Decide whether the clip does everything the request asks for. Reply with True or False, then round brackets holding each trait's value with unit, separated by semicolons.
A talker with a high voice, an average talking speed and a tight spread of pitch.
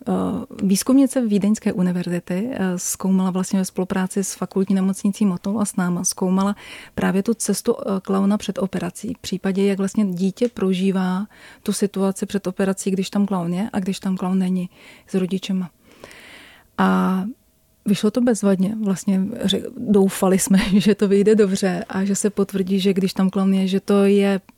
True (195 Hz; 160 wpm; 1.4 semitones)